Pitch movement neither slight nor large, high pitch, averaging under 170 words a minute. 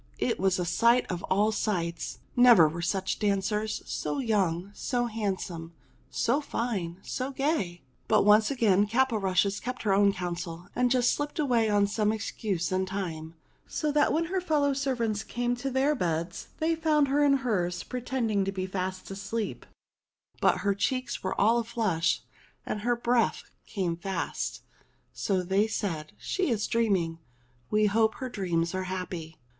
Yes: average, 4.8 semitones; high, 210 Hz; average, 160 wpm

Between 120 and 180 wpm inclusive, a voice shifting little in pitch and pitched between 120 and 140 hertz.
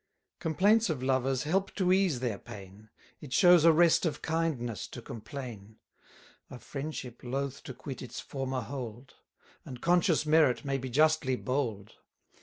No: average, 150 wpm; average, 4.5 semitones; low, 135 Hz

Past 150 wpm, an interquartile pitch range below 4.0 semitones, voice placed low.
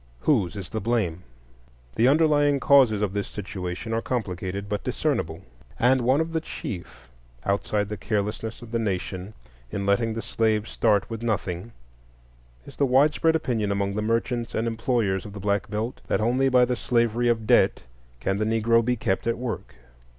Yes: average, 175 wpm; average, 3.3 semitones; low, 110 Hz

